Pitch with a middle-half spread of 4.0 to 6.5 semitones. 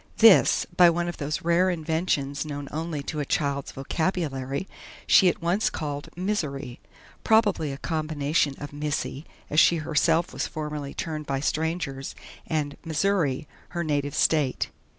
No: average, 3.1 semitones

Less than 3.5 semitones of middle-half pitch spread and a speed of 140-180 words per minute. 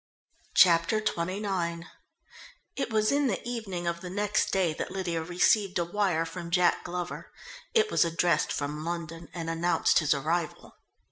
Yes: average, 2.7 semitones; average, 150 wpm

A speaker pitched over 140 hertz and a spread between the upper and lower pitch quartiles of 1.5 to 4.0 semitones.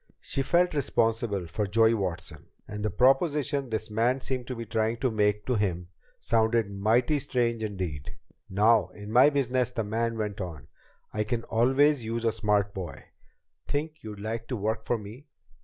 No: low, 115 Hz; average, 3.3 semitones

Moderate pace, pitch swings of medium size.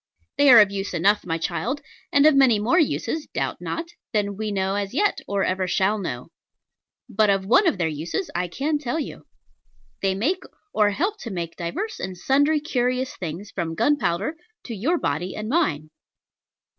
No: average, 180 wpm; wide, 7.5 semitones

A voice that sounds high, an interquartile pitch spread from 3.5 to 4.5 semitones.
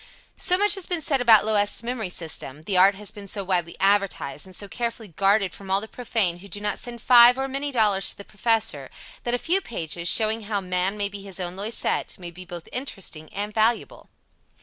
Yes: high, 205 Hz; average, 3.9 semitones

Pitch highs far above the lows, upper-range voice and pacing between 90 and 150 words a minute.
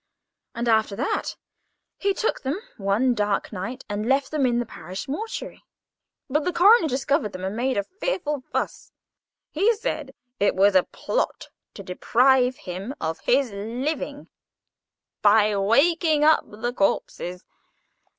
Yes: wide, 6.4 semitones; high, 245 Hz; average, 140 wpm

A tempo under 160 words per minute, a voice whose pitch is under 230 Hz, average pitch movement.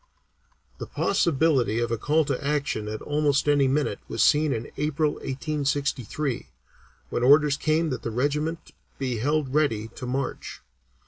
Yes: average, 145 wpm; medium, 140 Hz; average, 3.1 semitones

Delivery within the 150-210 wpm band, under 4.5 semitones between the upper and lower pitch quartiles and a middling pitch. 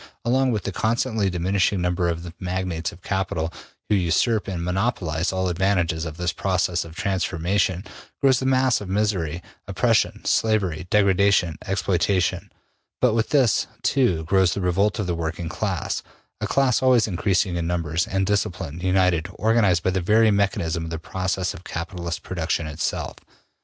No: average, 160 wpm; average, 3.2 semitones; very low, 95 Hz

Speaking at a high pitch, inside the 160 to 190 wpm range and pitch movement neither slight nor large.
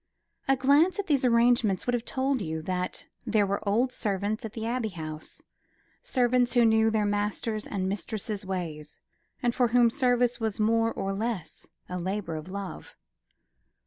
Yes: high, 220 Hz; average, 165 wpm; average, 3.9 semitones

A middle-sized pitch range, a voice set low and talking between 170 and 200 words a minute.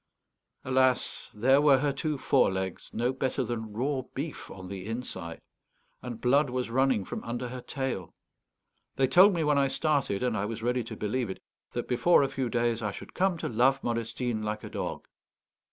Yes: average, 3.4 semitones; low, 125 Hz; average, 185 wpm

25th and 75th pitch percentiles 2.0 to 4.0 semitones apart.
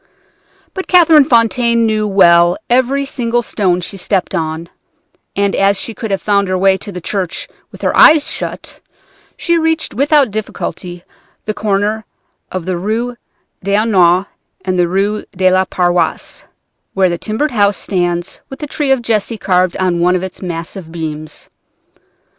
No: average, 4.4 semitones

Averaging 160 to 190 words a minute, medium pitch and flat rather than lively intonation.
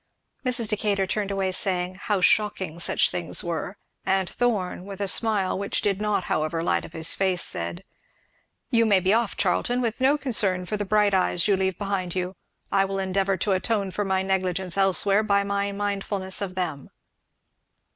No: average, 180 wpm; high, 195 Hz; narrow, 2.0 semitones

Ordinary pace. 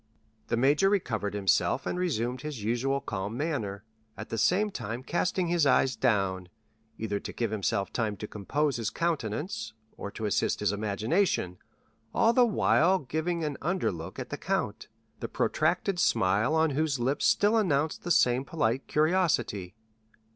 Yes: average, 160 wpm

